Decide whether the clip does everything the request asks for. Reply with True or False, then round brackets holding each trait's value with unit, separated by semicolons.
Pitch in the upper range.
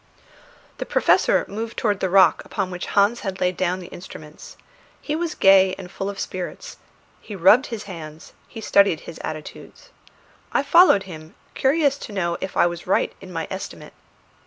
True (195 Hz)